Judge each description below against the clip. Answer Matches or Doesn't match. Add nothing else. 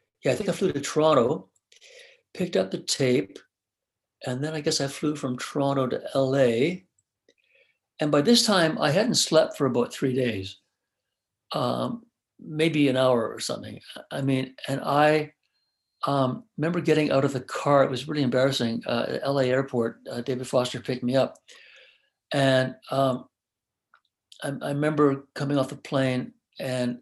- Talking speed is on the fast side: Doesn't match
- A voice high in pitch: Doesn't match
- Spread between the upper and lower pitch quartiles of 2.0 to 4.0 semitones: Matches